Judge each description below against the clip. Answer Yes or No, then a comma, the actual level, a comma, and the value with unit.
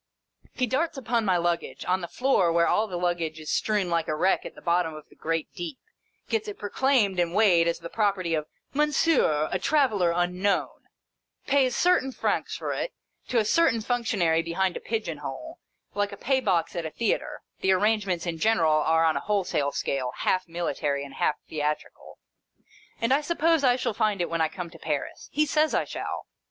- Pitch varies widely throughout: Yes, wide, 6.0 semitones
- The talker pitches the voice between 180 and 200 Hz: Yes, medium, 185 Hz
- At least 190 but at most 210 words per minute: Yes, fast, 205 wpm